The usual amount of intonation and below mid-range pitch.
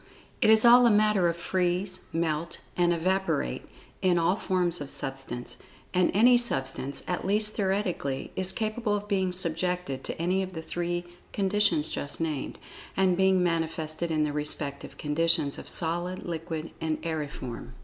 No: average, 3.2 semitones; medium, 175 Hz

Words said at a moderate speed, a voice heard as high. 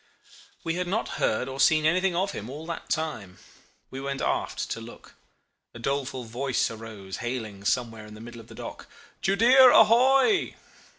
No: average, 170 wpm; low, 135 Hz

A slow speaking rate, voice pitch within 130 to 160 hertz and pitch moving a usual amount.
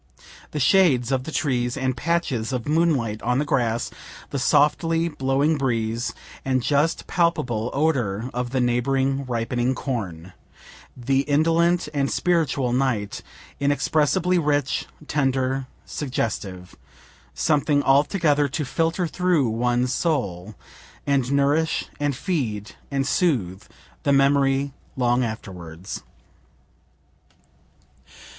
Yes: slow, 110 wpm; low, 135 Hz; average, 3.6 semitones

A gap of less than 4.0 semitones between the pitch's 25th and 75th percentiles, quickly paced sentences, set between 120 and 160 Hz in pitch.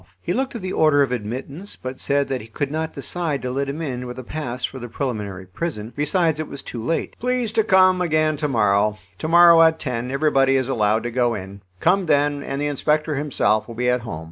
No: average, 4.6 semitones; fast, 235 wpm; medium, 140 Hz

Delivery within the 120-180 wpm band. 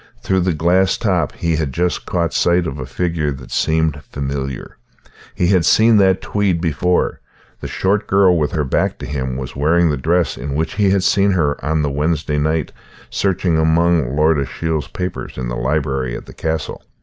No: average, 190 wpm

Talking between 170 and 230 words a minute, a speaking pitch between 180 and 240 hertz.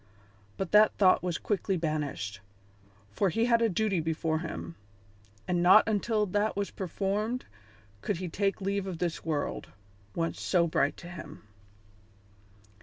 No: average, 145 wpm; medium, 185 Hz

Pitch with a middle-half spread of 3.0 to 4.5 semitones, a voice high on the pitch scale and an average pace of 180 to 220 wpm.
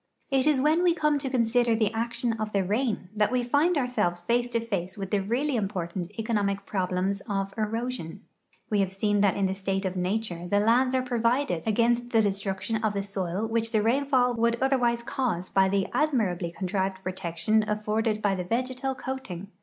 Yes: average, 4.0 semitones; high, 215 Hz; average, 190 wpm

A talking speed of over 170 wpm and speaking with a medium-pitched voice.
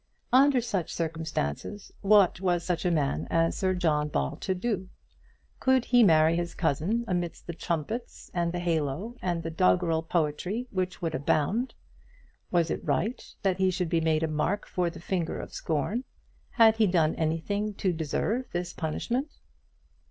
No: average, 165 wpm; medium, 175 Hz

